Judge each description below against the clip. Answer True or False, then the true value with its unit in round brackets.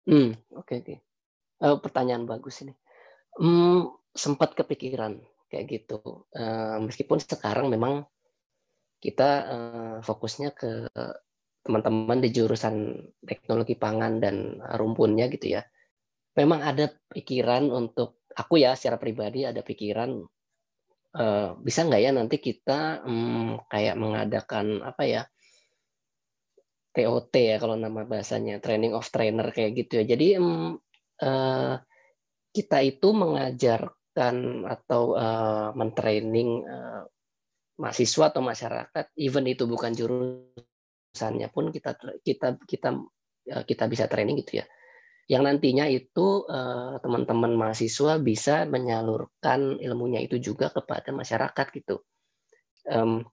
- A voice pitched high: False (120 Hz)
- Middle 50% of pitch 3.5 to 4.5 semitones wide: True (4.1 semitones)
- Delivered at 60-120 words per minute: True (110 wpm)